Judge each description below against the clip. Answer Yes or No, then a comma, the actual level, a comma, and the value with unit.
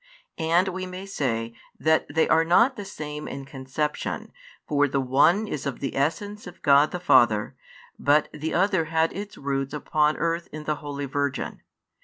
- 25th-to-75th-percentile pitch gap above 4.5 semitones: No, average, 3.7 semitones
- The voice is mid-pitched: Yes, medium, 150 Hz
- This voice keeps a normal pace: Yes, average, 175 wpm